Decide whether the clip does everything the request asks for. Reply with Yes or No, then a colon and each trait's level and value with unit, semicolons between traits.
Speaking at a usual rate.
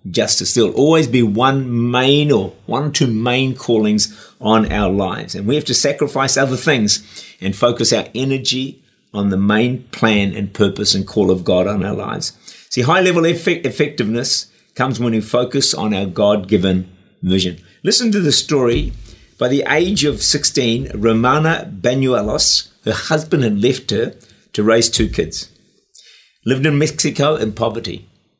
Yes: average, 165 wpm